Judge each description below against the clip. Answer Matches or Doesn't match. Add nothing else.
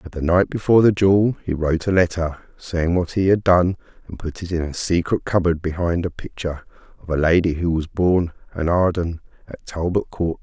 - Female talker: Doesn't match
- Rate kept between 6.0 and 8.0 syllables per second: Doesn't match